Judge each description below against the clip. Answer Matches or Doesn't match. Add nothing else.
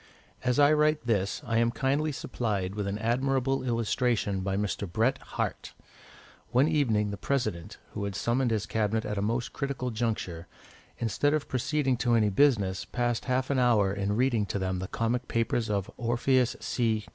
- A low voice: Matches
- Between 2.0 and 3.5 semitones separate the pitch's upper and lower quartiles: Doesn't match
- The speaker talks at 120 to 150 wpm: Doesn't match